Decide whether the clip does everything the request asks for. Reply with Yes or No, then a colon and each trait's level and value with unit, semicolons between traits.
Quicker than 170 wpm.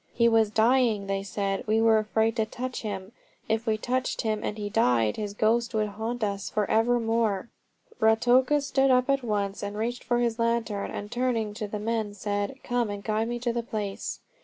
Yes: average, 200 wpm